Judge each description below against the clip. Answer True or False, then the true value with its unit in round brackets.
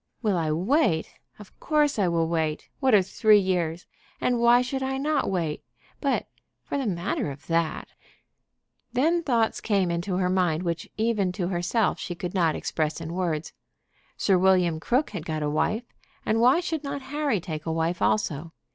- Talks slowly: False (180 wpm)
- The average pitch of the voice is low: False (185 Hz)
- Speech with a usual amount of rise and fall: False (6.3 semitones)